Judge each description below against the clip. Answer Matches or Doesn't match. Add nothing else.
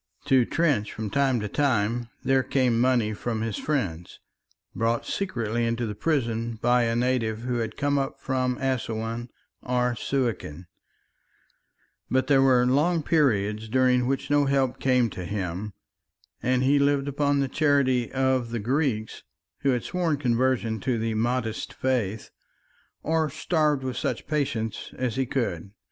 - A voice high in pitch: Doesn't match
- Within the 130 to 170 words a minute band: Matches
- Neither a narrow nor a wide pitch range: Matches